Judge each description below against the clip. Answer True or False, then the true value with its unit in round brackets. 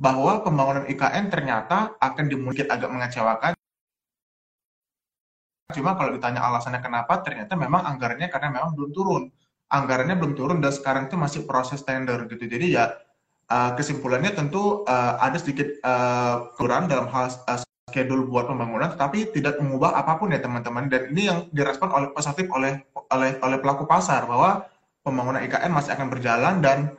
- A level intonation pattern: False (3.9 semitones)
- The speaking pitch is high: False (135 Hz)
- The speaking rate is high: True (150 wpm)